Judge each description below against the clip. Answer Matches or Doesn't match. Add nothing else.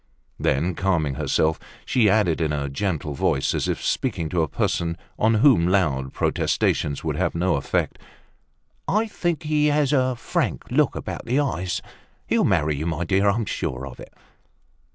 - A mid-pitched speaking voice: Doesn't match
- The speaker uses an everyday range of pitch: Doesn't match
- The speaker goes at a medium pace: Matches